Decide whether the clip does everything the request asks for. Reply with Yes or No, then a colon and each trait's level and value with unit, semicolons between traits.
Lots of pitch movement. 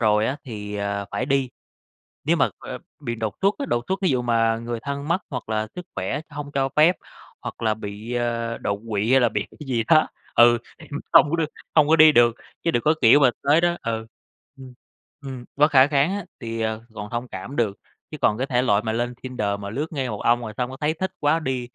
No: average, 4.4 semitones